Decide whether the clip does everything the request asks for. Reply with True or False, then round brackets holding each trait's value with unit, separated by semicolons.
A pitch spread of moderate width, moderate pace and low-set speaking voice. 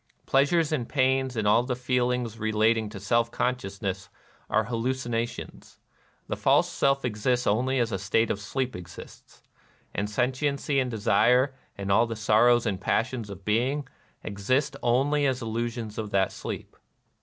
True (3.4 semitones; 155 wpm; 120 Hz)